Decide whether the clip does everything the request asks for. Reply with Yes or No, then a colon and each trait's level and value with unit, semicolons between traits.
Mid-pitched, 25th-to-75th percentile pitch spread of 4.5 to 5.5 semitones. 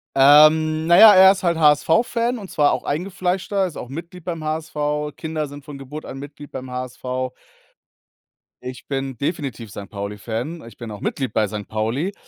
Yes: medium, 150 Hz; average, 5.0 semitones